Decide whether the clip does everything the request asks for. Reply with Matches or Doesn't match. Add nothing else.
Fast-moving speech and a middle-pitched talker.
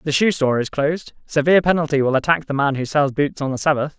Matches